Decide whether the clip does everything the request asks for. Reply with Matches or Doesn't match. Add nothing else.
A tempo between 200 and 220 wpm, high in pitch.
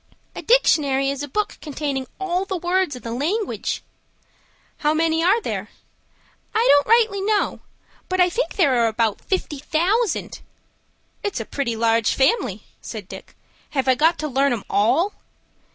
Doesn't match